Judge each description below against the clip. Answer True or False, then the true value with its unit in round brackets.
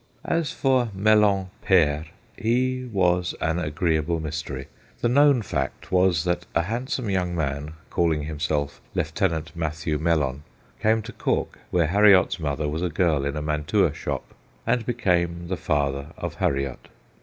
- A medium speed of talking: True (145 wpm)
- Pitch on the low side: True (85 Hz)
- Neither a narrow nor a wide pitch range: True (4.7 semitones)